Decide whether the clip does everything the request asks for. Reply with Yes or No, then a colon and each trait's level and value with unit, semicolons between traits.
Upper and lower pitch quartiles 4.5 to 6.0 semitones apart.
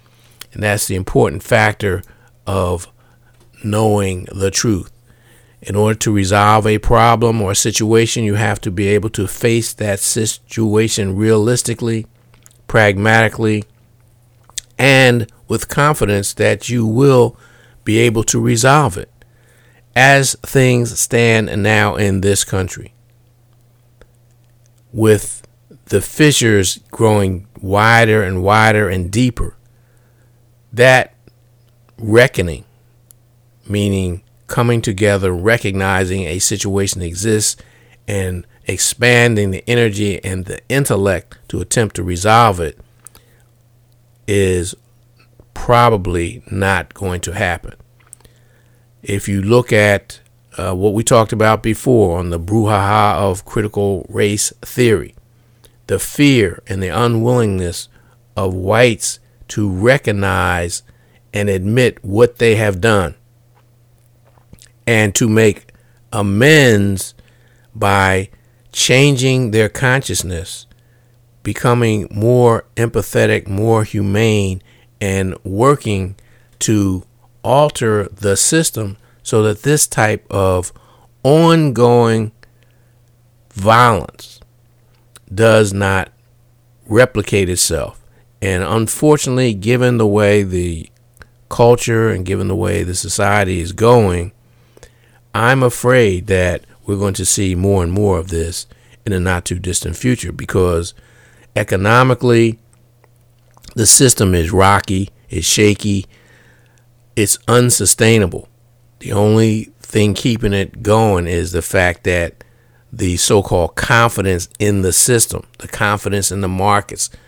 No: average, 3.1 semitones